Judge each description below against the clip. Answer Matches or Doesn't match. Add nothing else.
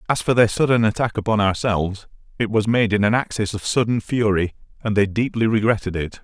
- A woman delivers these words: Doesn't match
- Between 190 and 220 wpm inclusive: Matches